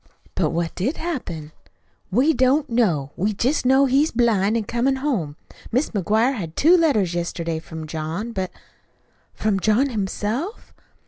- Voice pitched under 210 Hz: No, high, 220 Hz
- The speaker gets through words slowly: No, average, 150 wpm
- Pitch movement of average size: No, wide, 7.4 semitones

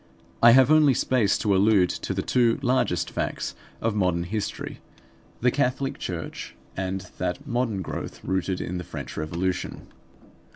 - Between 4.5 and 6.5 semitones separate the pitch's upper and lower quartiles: Yes, average, 5.3 semitones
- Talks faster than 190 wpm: No, average, 150 wpm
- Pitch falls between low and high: No, low, 105 Hz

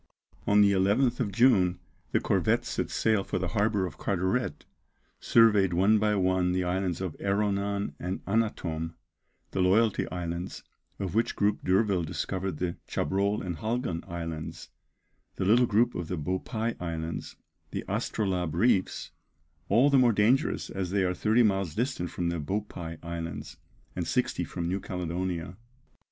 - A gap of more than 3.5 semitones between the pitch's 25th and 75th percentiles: No, average, 3.2 semitones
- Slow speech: No, average, 150 wpm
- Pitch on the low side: Yes, very low, 95 Hz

